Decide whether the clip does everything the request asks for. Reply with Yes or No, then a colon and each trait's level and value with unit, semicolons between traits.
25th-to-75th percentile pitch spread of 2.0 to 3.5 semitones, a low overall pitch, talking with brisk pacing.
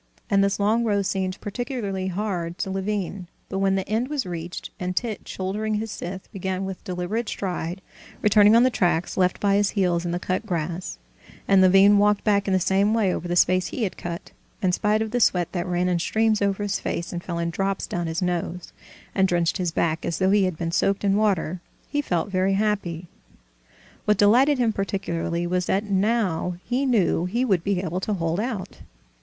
No: average, 2.7 semitones; high, 190 Hz; fast, 210 wpm